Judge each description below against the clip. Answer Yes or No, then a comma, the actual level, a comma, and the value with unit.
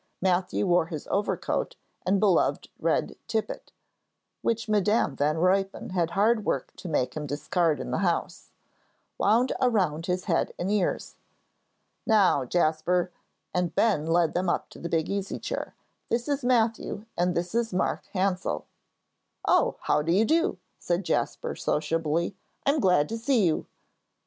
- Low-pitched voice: No, medium, 185 Hz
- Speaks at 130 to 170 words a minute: Yes, average, 150 wpm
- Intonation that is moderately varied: Yes, average, 4.4 semitones